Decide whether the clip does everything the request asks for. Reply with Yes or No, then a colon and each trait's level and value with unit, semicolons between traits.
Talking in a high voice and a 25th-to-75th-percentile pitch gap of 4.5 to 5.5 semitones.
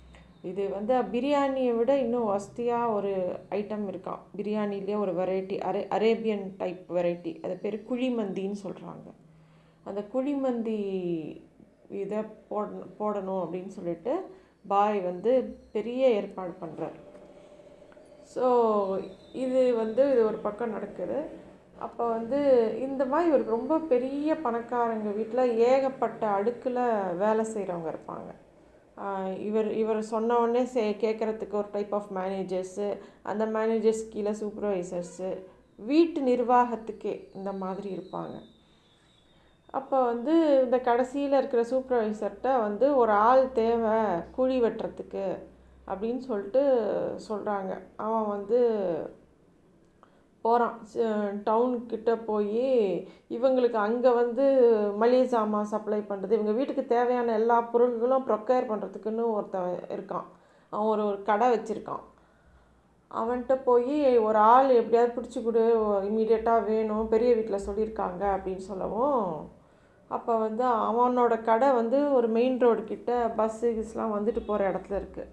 No: high, 220 Hz; average, 3.2 semitones